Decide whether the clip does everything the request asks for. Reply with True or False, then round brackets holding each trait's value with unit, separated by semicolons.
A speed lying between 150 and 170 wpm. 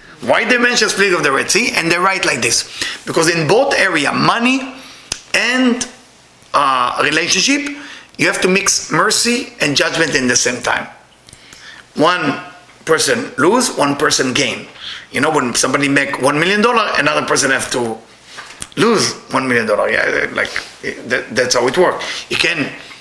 True (165 wpm)